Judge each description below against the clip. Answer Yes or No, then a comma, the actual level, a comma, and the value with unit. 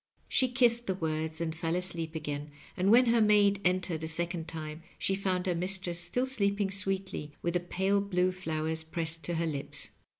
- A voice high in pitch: No, medium, 180 Hz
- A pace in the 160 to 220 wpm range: Yes, average, 190 wpm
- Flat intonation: No, average, 3.5 semitones